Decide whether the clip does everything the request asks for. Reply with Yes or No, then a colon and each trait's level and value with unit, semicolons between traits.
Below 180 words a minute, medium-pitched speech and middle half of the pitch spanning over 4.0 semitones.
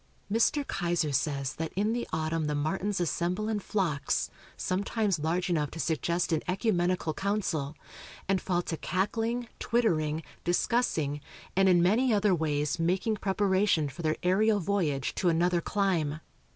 Yes: average, 145 wpm; medium, 180 Hz; average, 4.4 semitones